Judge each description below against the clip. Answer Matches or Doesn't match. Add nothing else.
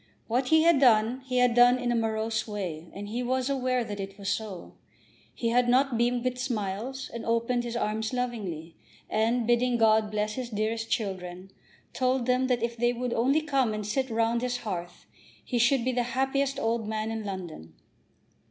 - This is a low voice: Doesn't match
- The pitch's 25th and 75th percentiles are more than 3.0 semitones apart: Doesn't match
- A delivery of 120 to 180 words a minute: Doesn't match